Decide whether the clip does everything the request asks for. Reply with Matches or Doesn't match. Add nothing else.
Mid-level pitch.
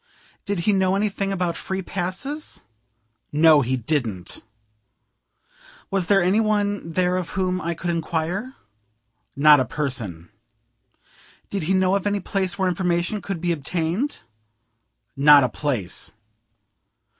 Matches